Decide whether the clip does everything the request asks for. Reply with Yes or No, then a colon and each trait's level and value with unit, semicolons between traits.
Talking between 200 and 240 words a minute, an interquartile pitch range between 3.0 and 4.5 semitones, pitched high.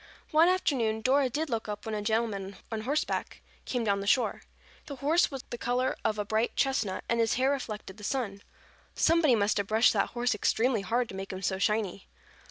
Yes: fast, 205 wpm; average, 4.0 semitones; high, 225 Hz